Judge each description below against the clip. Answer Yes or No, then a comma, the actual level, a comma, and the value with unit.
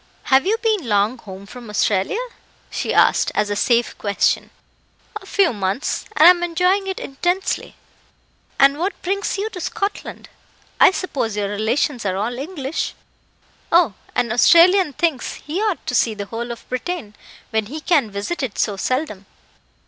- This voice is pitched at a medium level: No, very high, 265 Hz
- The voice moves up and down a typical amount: No, wide, 8.8 semitones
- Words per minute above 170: No, average, 160 wpm